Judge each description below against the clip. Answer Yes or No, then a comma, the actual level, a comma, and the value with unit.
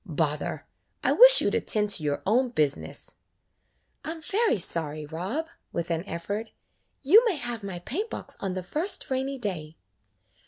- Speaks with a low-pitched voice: No, high, 205 Hz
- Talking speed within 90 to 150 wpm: No, average, 165 wpm